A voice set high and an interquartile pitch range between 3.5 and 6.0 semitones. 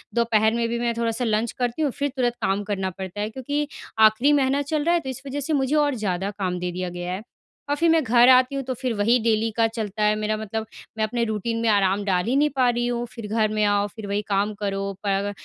Yes: high, 225 Hz; average, 3.9 semitones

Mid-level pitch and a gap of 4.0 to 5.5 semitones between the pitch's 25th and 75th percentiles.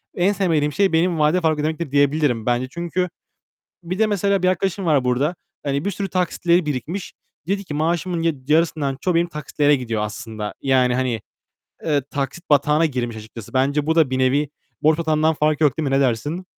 Yes: medium, 150 Hz; average, 4.3 semitones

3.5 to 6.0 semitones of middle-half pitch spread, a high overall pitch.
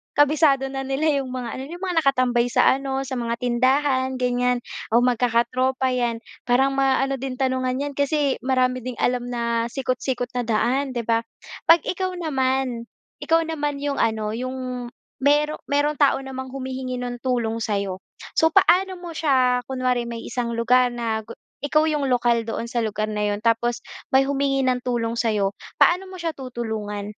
No: narrow, 2.5 semitones; very high, 255 Hz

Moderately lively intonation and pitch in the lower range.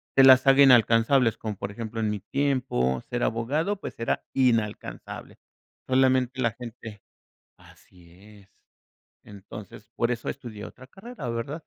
Yes: average, 3.7 semitones; low, 120 Hz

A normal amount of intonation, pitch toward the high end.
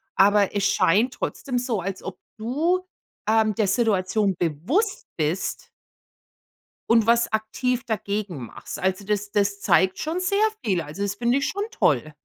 Yes: average, 4.2 semitones; high, 210 Hz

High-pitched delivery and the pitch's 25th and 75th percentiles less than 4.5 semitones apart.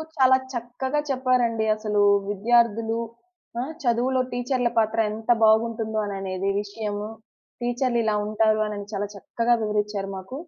Yes: high, 225 Hz; narrow, 2.5 semitones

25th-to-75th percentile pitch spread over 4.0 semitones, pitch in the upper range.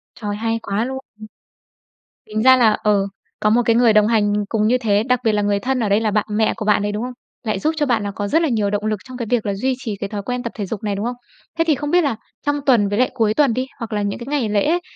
No: average, 3.4 semitones; high, 220 Hz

